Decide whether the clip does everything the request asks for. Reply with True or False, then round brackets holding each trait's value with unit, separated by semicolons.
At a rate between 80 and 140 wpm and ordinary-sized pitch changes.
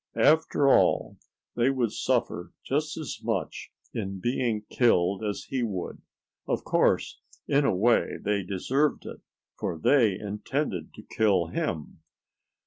False (135 wpm; 5.7 semitones)